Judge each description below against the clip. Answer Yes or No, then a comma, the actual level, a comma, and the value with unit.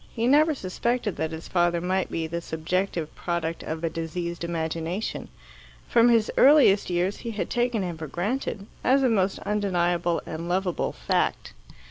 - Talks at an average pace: Yes, average, 160 wpm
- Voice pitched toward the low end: No, medium, 180 Hz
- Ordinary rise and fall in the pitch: Yes, average, 4.5 semitones